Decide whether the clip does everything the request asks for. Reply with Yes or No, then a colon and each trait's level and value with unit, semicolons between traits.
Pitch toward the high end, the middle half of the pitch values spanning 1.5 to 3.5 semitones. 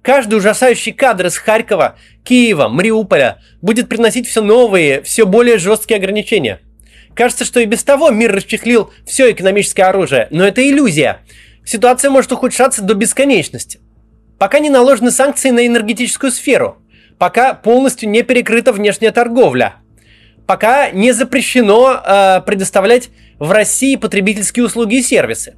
No: high, 230 Hz; average, 3.9 semitones